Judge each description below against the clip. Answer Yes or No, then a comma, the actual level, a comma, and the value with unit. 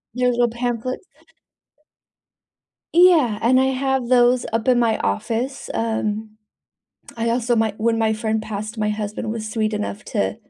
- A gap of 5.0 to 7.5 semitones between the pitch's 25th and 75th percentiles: No, narrow, 2.4 semitones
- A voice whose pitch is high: Yes, high, 230 Hz